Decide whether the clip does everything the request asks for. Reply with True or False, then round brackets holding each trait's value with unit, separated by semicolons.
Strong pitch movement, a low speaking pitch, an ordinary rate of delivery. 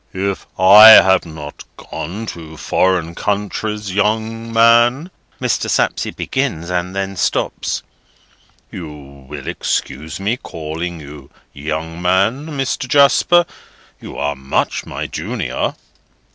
False (6.0 semitones; 95 Hz; 110 wpm)